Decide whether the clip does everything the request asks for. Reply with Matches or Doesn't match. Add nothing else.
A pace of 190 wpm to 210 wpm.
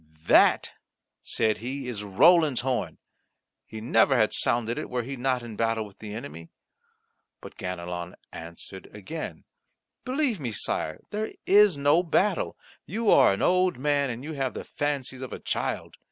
Doesn't match